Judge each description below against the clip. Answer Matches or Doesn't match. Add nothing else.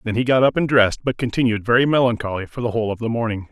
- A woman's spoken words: Doesn't match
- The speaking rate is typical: Doesn't match